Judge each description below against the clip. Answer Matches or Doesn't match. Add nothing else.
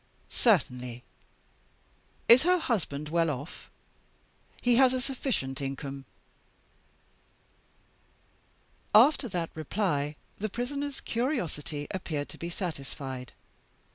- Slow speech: Matches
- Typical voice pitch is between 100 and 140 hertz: Doesn't match